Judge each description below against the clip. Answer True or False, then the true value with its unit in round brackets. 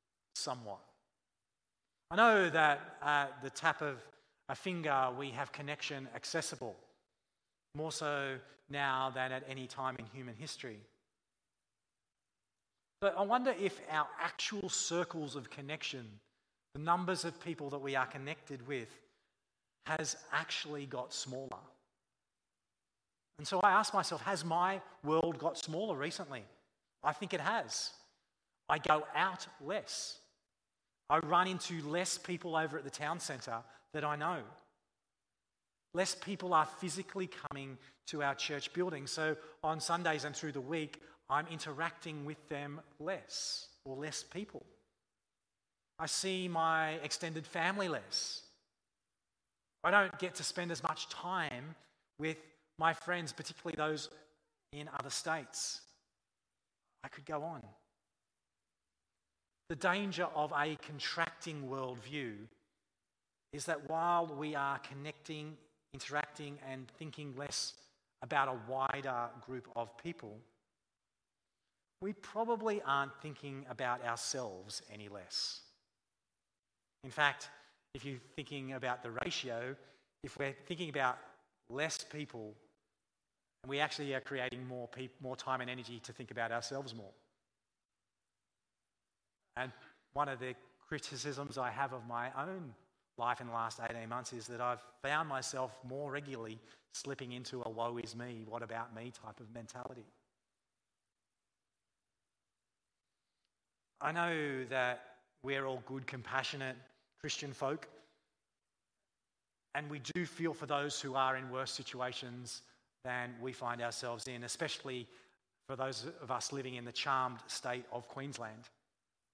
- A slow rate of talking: True (130 wpm)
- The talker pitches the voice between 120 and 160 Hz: True (140 Hz)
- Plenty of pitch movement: False (4.2 semitones)